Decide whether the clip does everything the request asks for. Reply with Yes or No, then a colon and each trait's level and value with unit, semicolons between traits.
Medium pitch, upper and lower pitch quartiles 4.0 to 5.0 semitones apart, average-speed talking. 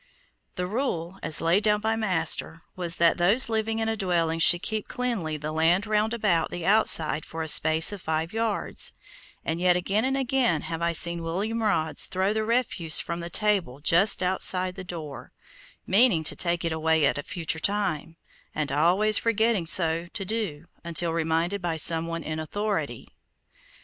Yes: medium, 175 Hz; average, 4.4 semitones; average, 180 wpm